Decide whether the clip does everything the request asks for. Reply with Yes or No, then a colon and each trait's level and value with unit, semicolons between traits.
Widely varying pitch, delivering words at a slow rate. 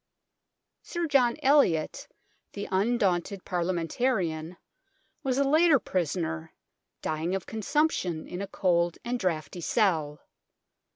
Yes: wide, 6.6 semitones; slow, 115 wpm